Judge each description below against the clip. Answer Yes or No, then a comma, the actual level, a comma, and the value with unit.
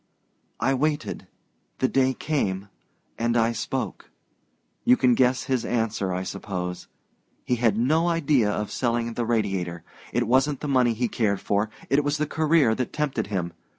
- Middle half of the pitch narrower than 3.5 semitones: No, average, 4.4 semitones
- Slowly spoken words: No, average, 160 wpm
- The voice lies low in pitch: Yes, low, 120 Hz